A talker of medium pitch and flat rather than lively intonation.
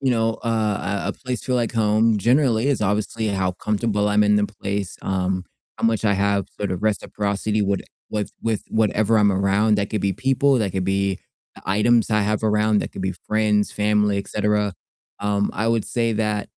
No: low, 105 Hz; narrow, 1.8 semitones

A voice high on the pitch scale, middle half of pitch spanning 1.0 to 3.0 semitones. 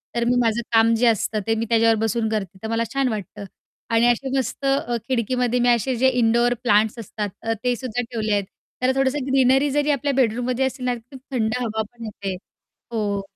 Yes: high, 235 Hz; narrow, 2.5 semitones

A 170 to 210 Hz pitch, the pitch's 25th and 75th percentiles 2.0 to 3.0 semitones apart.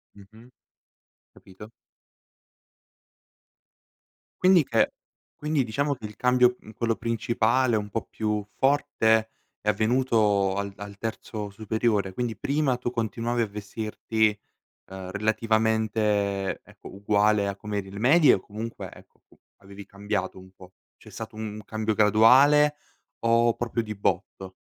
No: low, 110 Hz; narrow, 2.4 semitones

